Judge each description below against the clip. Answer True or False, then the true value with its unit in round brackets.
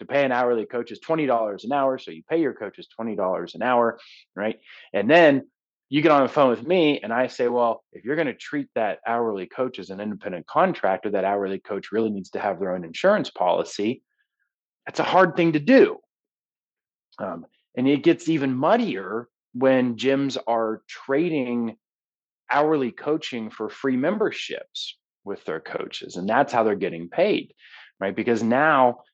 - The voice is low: True (125 Hz)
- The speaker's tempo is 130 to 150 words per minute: False (180 wpm)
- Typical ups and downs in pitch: True (3.8 semitones)